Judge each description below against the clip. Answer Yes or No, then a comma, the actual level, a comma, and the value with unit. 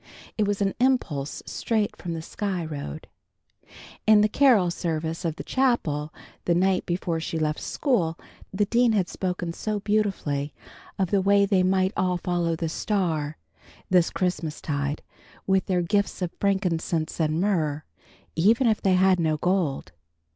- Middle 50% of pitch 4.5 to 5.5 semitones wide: No, average, 3.9 semitones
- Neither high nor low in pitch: Yes, medium, 180 Hz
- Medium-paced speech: Yes, average, 155 wpm